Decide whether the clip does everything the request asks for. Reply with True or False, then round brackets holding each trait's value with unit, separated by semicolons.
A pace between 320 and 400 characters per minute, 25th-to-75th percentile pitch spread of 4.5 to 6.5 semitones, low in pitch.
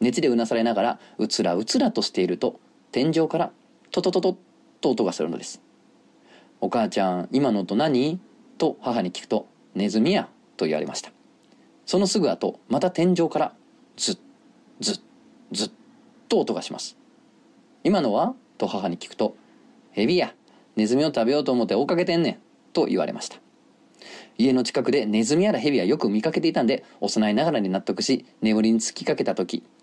False (340 characters per minute; 7.4 semitones; 115 Hz)